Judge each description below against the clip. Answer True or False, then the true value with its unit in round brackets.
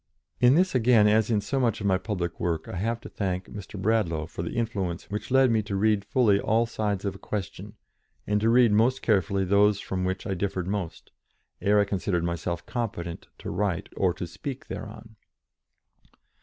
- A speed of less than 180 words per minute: False (195 wpm)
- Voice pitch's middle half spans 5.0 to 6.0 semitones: False (3.2 semitones)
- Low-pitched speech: True (100 Hz)